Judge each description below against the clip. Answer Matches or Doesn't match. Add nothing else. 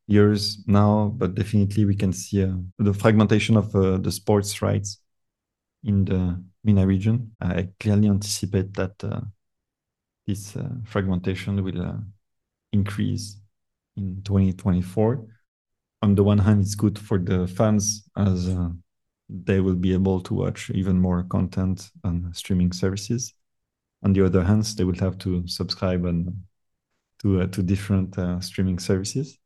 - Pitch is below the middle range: Matches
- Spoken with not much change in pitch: Matches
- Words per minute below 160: Matches